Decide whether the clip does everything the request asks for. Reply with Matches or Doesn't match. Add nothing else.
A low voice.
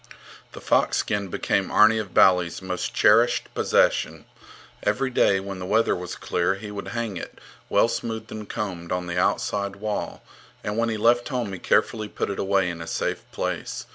Matches